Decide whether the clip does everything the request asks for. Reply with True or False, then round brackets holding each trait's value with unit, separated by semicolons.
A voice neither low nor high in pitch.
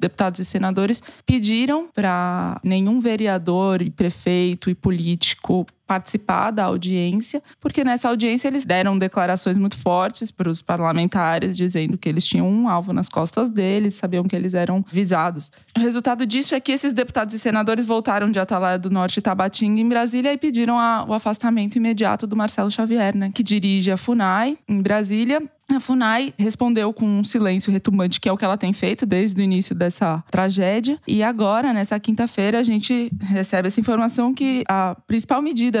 False (205 Hz)